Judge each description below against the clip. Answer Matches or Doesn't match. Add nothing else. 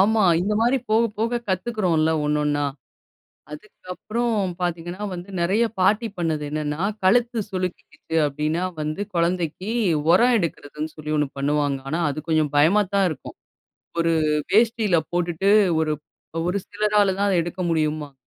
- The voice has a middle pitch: Matches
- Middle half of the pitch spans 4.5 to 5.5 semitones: Matches